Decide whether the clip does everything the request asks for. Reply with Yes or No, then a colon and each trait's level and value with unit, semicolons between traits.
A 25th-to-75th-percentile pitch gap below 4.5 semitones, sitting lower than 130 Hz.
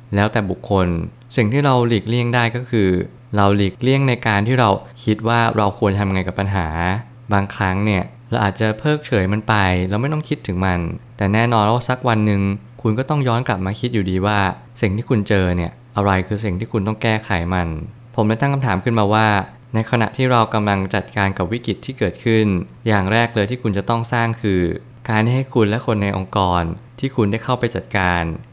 Yes: average, 3.4 semitones; low, 110 Hz